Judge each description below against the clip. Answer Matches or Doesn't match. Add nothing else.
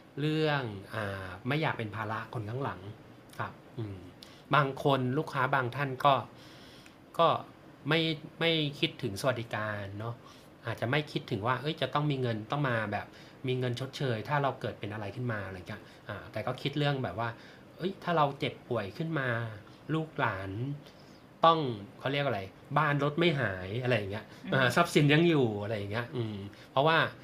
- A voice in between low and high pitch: Doesn't match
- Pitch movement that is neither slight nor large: Matches